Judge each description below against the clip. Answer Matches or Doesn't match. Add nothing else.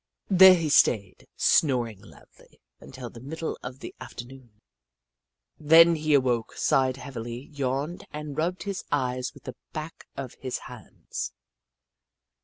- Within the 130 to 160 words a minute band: Matches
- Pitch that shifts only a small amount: Doesn't match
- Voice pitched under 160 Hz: Matches